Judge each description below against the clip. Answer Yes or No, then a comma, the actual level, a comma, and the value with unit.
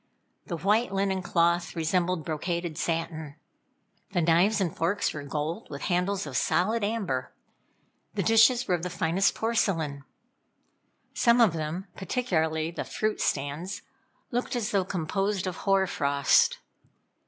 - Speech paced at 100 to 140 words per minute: Yes, slow, 135 wpm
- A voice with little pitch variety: No, average, 3.8 semitones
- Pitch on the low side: No, medium, 180 Hz